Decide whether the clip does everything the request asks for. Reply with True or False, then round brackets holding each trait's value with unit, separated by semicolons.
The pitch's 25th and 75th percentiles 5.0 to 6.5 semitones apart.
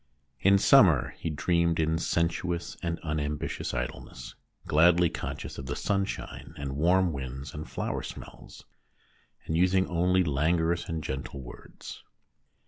False (3.2 semitones)